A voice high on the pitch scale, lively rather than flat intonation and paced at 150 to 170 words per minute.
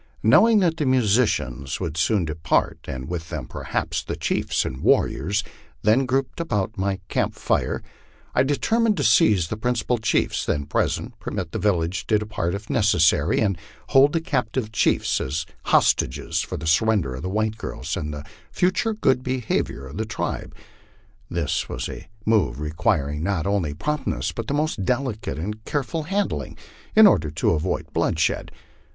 No: low, 105 Hz; wide, 7.9 semitones; average, 165 wpm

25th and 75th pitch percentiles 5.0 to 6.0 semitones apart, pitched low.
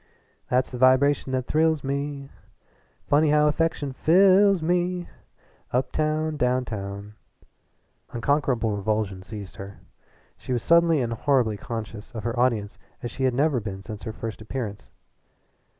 Yes: wide, 5.5 semitones; low, 130 Hz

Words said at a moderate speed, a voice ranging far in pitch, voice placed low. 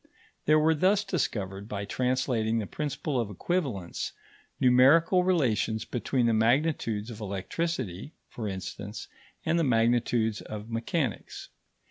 No: slow, 120 wpm; wide, 6.1 semitones; low, 120 Hz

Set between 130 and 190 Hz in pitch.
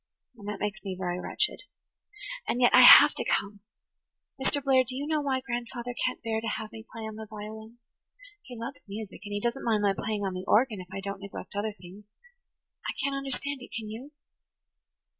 No: high, 220 Hz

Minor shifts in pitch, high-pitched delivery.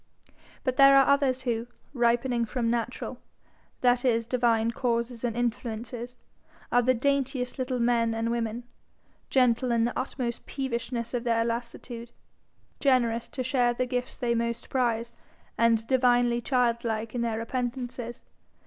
Yes: narrow, 1.5 semitones; high, 240 Hz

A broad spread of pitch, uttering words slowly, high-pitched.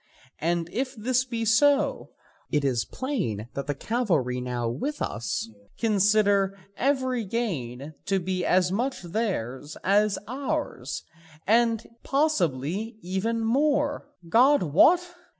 Yes: wide, 8.3 semitones; slow, 115 wpm; high, 210 Hz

